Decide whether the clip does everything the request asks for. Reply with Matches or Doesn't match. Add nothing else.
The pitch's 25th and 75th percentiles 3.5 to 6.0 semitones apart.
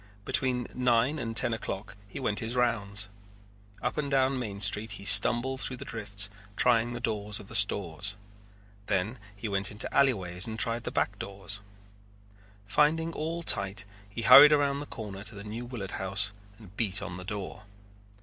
Matches